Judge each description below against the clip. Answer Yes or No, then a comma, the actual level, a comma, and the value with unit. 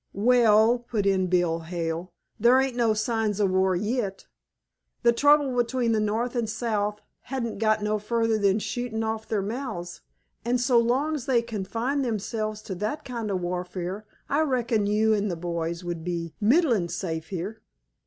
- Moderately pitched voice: No, high, 215 Hz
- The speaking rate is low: No, average, 165 wpm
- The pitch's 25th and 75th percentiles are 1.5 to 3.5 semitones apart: No, average, 4.1 semitones